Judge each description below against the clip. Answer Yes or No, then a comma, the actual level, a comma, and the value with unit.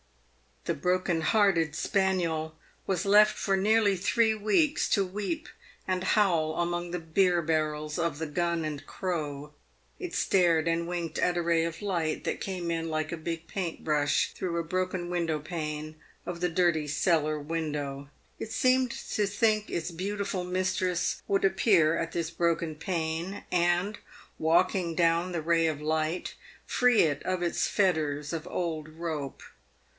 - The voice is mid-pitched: Yes, medium, 170 Hz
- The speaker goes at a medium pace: Yes, average, 155 wpm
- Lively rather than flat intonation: No, average, 3.0 semitones